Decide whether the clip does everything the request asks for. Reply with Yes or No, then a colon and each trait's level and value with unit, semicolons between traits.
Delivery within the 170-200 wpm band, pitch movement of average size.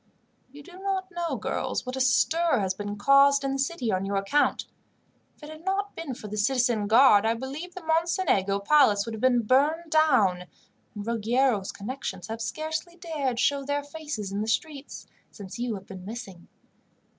No: average, 190 wpm; wide, 6.9 semitones